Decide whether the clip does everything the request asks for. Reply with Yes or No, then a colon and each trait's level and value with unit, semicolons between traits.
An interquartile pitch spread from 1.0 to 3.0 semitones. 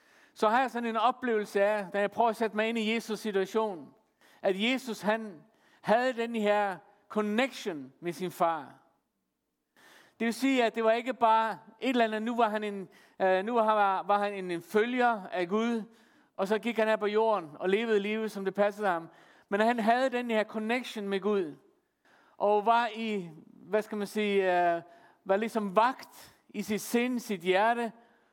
Yes: narrow, 2.5 semitones